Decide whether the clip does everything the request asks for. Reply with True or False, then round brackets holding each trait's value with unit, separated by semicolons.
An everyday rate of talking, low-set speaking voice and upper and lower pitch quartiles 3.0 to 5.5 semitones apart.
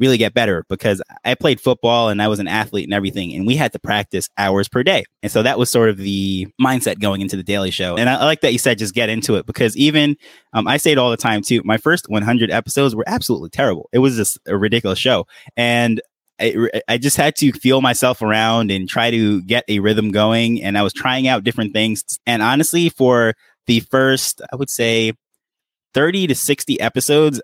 False (225 wpm; 115 Hz; 3.4 semitones)